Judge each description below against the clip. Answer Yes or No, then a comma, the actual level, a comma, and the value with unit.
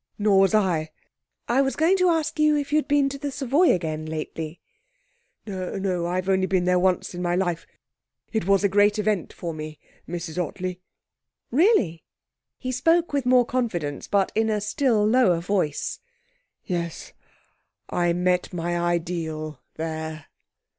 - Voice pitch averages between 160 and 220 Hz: Yes, high, 190 Hz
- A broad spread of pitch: Yes, wide, 6.5 semitones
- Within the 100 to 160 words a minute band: Yes, average, 155 wpm